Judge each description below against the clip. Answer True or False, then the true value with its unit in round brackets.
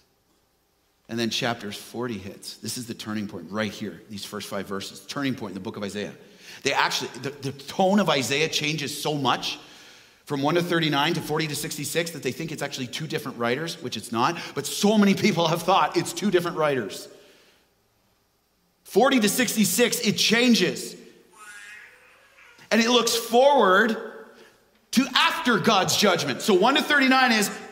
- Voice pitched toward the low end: False (155 Hz)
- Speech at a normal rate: True (175 wpm)